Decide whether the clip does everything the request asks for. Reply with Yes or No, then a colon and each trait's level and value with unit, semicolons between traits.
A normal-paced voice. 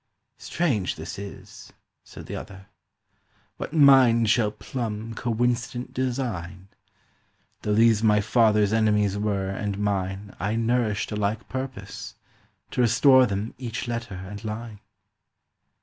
No: slow, 120 wpm